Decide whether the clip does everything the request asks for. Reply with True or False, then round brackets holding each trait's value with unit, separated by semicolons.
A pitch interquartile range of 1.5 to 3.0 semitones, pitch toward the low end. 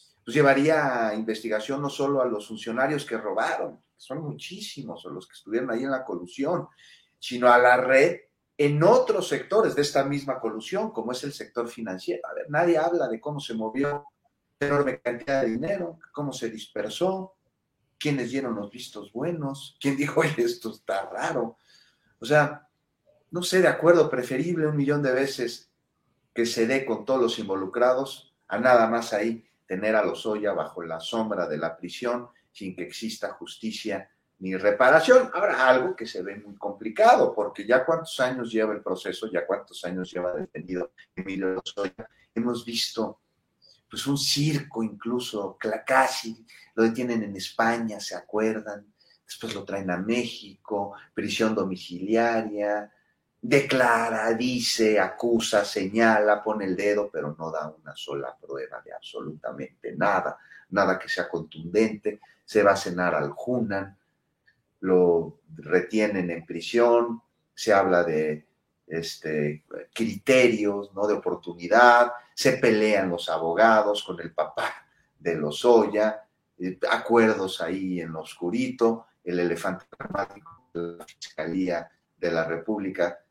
False (5.1 semitones; 115 Hz)